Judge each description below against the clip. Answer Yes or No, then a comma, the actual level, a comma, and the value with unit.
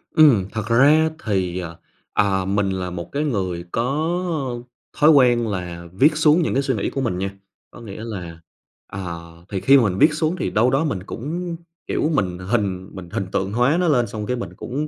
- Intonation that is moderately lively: No, wide, 7.2 semitones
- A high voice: No, low, 115 Hz